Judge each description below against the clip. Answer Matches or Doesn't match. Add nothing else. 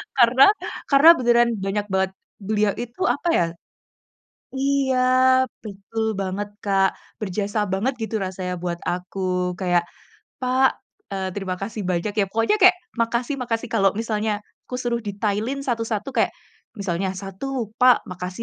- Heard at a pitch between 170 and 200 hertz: Doesn't match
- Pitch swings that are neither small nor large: Matches